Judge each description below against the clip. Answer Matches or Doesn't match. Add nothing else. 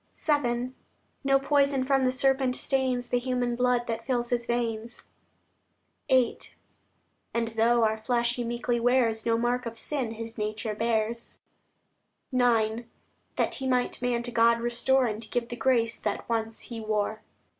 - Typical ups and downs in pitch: Doesn't match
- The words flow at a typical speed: Matches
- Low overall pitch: Doesn't match